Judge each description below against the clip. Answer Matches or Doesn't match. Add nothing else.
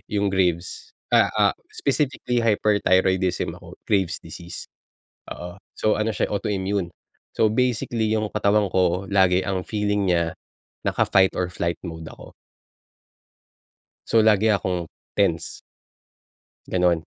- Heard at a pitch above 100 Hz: Doesn't match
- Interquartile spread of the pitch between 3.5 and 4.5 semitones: Doesn't match